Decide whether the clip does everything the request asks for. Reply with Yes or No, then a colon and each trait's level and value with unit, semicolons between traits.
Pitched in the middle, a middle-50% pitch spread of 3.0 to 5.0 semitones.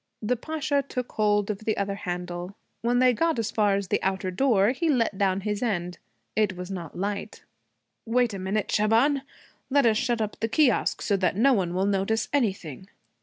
No: high, 210 Hz; average, 4.2 semitones